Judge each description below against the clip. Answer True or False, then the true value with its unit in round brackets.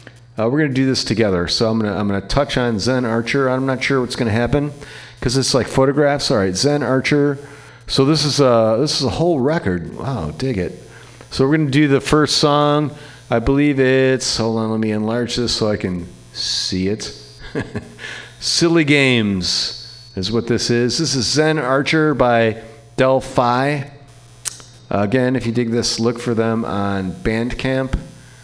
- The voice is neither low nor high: False (125 Hz)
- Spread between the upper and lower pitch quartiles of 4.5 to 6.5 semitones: False (3.8 semitones)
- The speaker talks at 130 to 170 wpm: False (180 wpm)